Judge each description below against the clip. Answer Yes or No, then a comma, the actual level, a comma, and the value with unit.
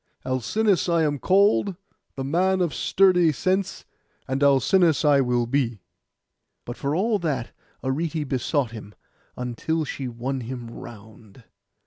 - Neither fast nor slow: No, slow, 130 wpm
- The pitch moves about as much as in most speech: No, wide, 5.9 semitones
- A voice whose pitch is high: No, medium, 140 Hz